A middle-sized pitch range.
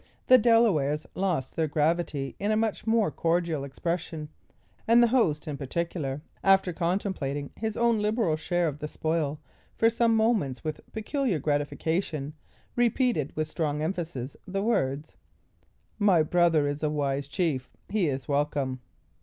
No: wide, 5.9 semitones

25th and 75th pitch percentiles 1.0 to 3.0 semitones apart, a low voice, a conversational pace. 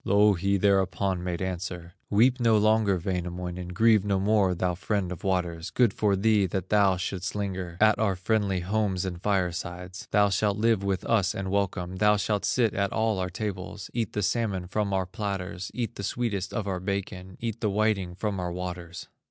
Yes: narrow, 2.5 semitones; very low, 95 Hz; average, 185 wpm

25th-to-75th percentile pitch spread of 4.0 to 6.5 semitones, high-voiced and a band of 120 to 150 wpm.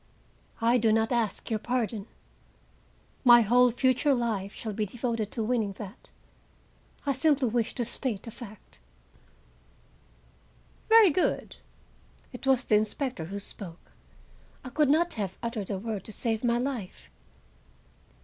No: average, 3.1 semitones; high, 230 Hz; average, 140 wpm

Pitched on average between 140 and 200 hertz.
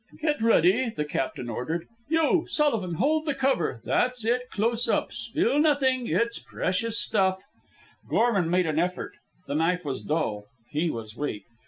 Yes: high, 190 Hz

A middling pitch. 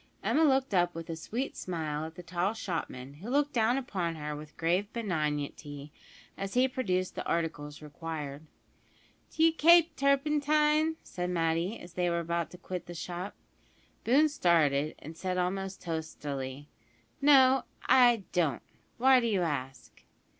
Yes: medium, 180 Hz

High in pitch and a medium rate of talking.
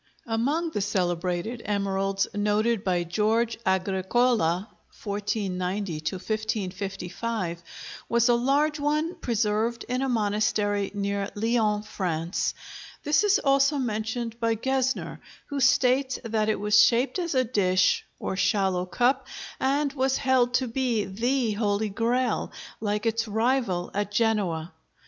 No: high, 220 Hz; slow, 125 wpm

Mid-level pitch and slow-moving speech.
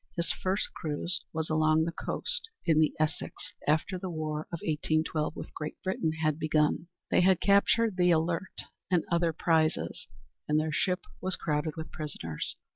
No: medium, 160 Hz; average, 165 wpm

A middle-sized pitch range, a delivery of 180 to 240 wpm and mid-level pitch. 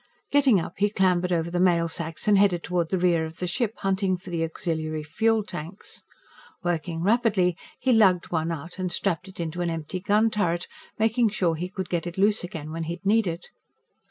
Yes: average, 3.2 semitones; fast, 205 wpm; medium, 180 Hz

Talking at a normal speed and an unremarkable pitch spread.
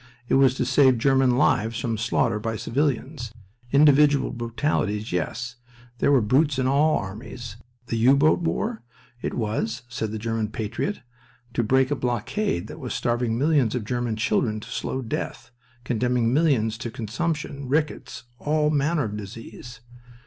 Yes: average, 155 wpm; average, 3.8 semitones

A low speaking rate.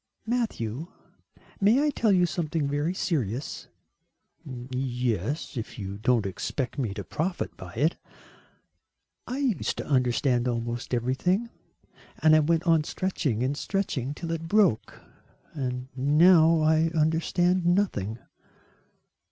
Yes: slow, 120 wpm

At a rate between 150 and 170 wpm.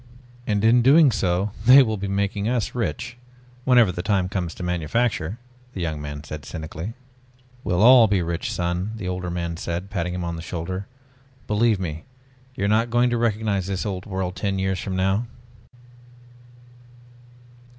Yes: average, 165 wpm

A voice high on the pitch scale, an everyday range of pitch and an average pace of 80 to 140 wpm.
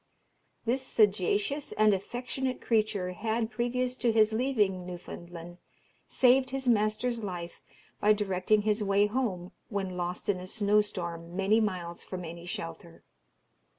Yes: high, 210 Hz; average, 4.2 semitones; slow, 135 wpm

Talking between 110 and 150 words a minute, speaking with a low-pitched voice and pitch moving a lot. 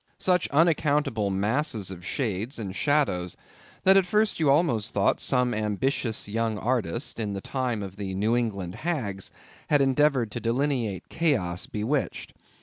Yes: average, 145 wpm; low, 115 Hz; wide, 6.0 semitones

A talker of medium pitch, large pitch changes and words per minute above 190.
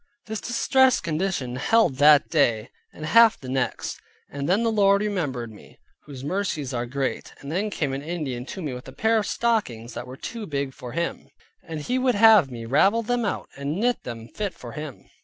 Yes: medium, 155 Hz; wide, 8.2 semitones; average, 200 wpm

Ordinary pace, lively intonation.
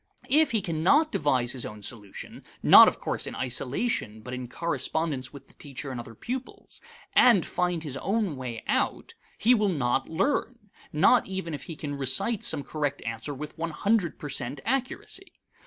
Yes: average, 175 wpm; wide, 7.6 semitones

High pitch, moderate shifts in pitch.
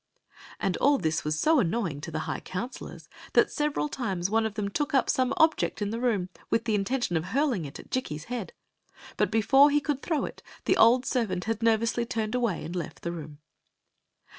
No: high, 225 Hz; wide, 6.1 semitones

